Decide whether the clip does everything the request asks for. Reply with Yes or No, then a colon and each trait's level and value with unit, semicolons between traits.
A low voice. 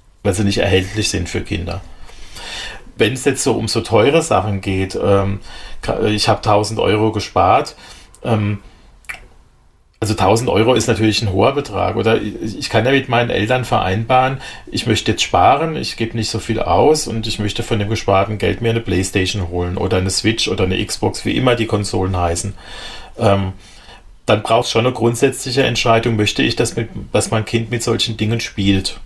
Yes: low, 110 Hz